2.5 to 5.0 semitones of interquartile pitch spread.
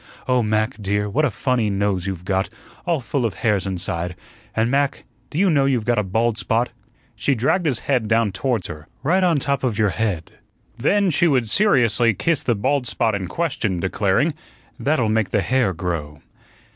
No: wide, 5.4 semitones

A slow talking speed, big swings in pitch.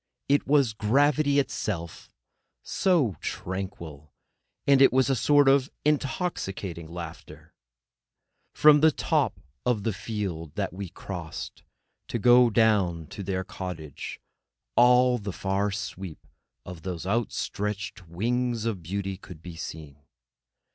Yes: slow, 115 wpm; wide, 6.0 semitones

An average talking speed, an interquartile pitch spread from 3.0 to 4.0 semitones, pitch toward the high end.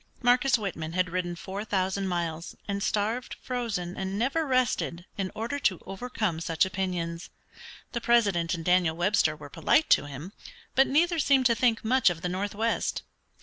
No: average, 165 wpm; average, 5.3 semitones; high, 195 Hz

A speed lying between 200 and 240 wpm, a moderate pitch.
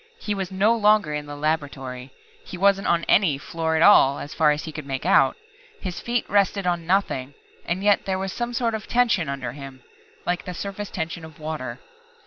Yes: fast, 205 wpm; medium, 170 Hz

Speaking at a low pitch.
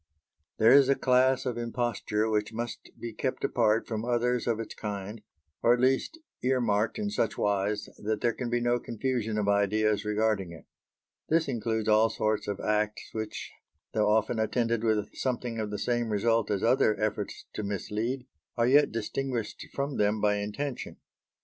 Yes: low, 110 Hz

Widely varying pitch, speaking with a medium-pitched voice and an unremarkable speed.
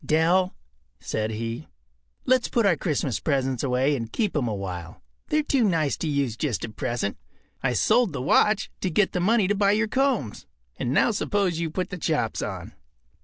Yes: wide, 8.8 semitones; medium, 160 Hz; average, 190 wpm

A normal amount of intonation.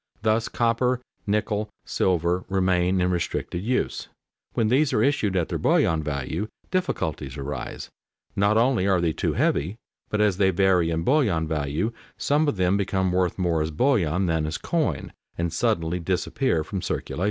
Yes: average, 4.8 semitones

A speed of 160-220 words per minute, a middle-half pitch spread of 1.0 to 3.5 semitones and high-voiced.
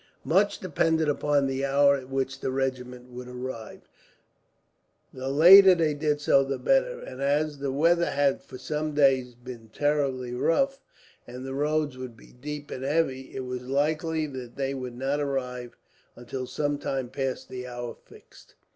No: average, 165 wpm; average, 2.7 semitones; low, 135 Hz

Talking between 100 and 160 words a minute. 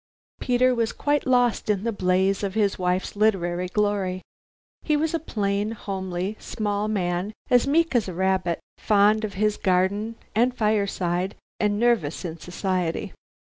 Yes: average, 150 wpm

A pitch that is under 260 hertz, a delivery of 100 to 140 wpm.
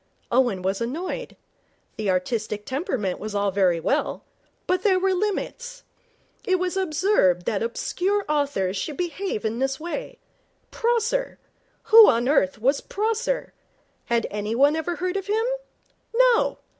No: very high, 305 Hz; slow, 135 wpm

